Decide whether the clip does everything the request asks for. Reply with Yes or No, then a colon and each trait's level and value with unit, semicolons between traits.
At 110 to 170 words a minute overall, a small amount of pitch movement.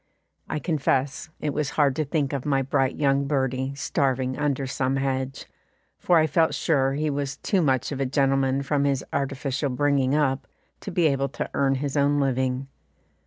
No: average, 180 wpm; narrow, 1.5 semitones